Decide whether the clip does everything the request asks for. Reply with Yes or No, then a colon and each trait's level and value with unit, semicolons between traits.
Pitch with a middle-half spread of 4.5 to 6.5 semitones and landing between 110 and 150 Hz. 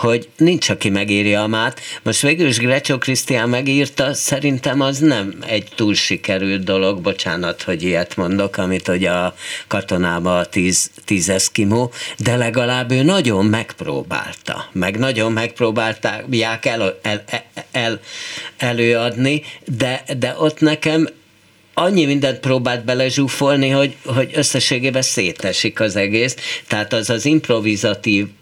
Yes: average, 4.8 semitones; low, 120 Hz